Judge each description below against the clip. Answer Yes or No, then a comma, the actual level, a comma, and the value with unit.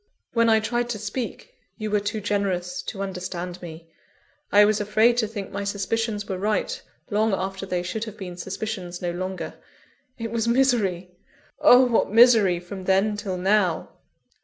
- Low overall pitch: No, high, 205 Hz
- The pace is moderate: Yes, average, 170 wpm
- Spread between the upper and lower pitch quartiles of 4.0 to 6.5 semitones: No, average, 3.2 semitones